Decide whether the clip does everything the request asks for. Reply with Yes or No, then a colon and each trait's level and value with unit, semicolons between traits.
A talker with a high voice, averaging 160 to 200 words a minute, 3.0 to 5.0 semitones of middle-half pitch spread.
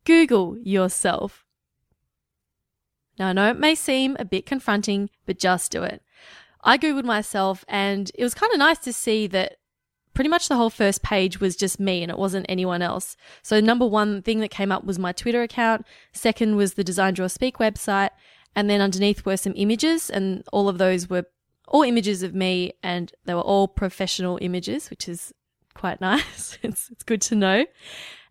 Yes: high, 200 Hz; average, 185 wpm; average, 3.5 semitones